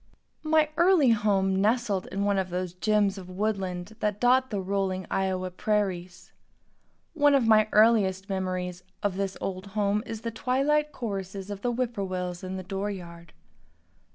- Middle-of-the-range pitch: No, high, 200 Hz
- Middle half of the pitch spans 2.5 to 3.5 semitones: Yes, average, 3.2 semitones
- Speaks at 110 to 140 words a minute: No, average, 155 wpm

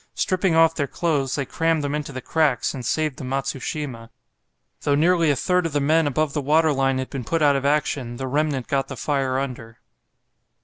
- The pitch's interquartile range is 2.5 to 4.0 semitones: Yes, average, 2.8 semitones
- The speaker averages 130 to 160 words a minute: No, fast, 205 wpm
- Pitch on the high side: No, medium, 145 Hz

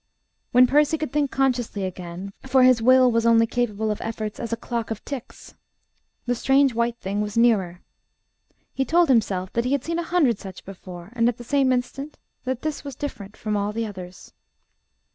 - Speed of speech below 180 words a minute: No, average, 190 wpm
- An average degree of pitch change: Yes, average, 4.3 semitones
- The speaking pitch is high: Yes, high, 235 Hz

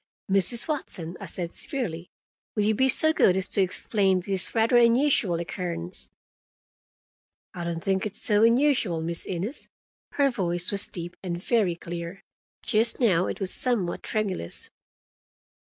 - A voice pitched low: No, high, 190 Hz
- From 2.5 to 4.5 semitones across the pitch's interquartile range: No, average, 4.9 semitones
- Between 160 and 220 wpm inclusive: No, average, 145 wpm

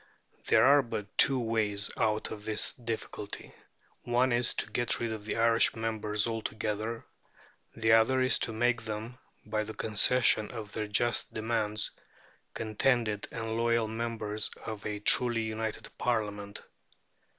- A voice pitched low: Yes, low, 110 Hz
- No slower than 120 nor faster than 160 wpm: Yes, average, 140 wpm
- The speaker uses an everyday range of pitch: No, narrow, 1.6 semitones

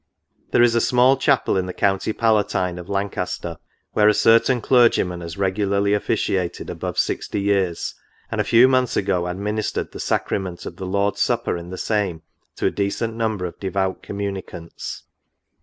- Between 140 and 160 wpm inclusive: No, average, 170 wpm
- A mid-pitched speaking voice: No, low, 100 Hz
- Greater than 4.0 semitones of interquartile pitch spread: No, average, 3.1 semitones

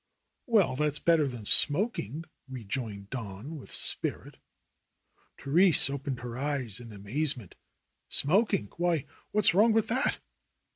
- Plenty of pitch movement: Yes, wide, 6.4 semitones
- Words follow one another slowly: Yes, slow, 115 wpm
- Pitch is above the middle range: No, medium, 140 Hz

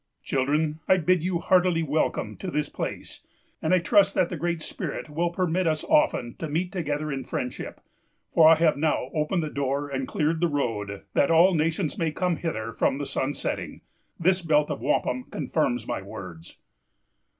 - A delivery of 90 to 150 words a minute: No, average, 180 wpm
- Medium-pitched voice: Yes, medium, 155 Hz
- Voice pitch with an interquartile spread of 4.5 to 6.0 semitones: No, average, 3.6 semitones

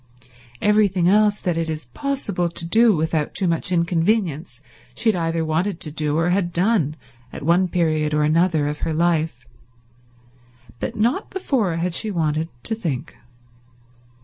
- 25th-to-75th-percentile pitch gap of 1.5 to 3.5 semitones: No, average, 4.1 semitones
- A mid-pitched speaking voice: Yes, medium, 170 Hz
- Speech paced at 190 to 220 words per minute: No, average, 155 wpm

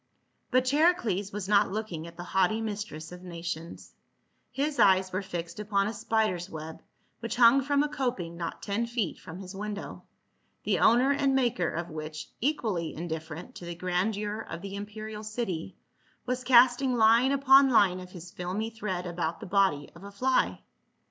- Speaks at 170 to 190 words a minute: Yes, average, 175 wpm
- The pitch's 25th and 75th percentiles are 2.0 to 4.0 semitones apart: No, average, 5.1 semitones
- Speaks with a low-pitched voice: No, high, 200 Hz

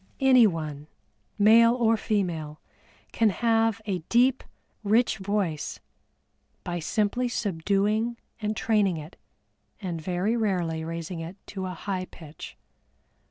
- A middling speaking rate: No, slow, 115 wpm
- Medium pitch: No, high, 200 Hz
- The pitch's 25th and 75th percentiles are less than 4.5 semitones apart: No, average, 5.0 semitones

